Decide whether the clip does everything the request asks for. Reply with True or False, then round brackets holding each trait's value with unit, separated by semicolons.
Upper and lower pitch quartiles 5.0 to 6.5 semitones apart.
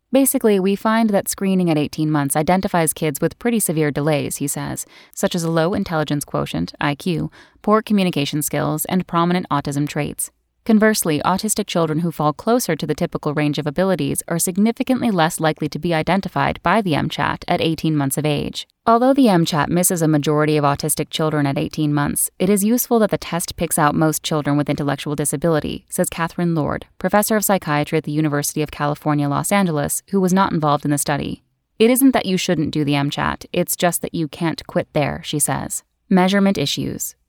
False (4.2 semitones)